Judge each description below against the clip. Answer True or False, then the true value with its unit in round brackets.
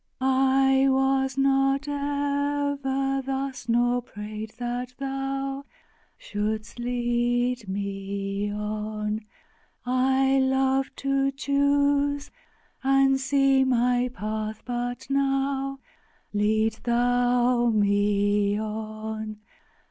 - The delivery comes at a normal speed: False (85 wpm)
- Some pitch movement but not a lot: True (3.9 semitones)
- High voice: True (250 Hz)